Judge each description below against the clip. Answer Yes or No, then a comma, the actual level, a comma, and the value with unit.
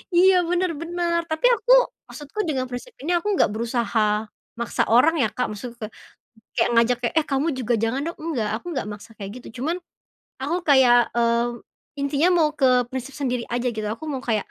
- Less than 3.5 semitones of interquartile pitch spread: No, wide, 5.5 semitones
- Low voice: No, very high, 260 Hz